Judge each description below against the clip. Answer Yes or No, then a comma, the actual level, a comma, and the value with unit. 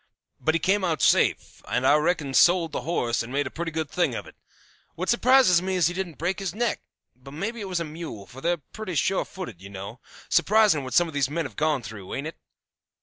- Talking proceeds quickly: Yes, fast, 240 wpm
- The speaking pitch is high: No, medium, 165 Hz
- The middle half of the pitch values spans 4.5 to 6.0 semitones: Yes, average, 5.1 semitones